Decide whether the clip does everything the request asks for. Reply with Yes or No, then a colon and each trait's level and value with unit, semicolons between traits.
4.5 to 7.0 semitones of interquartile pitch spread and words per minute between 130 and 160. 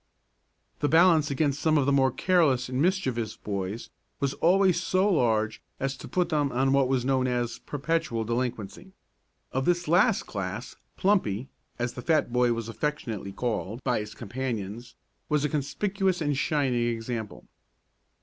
Yes: average, 5.2 semitones; average, 155 wpm